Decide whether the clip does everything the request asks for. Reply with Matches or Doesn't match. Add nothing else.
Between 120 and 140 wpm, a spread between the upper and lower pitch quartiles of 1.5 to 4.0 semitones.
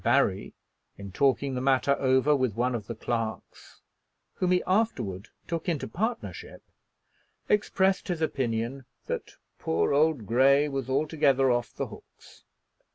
Doesn't match